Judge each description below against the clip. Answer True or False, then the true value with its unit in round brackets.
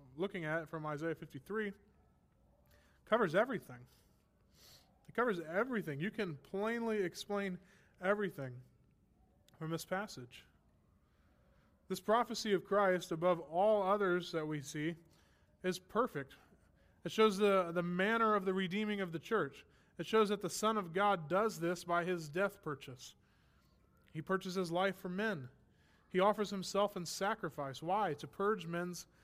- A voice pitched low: False (180 Hz)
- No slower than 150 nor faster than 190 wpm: False (140 wpm)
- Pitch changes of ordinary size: True (4.5 semitones)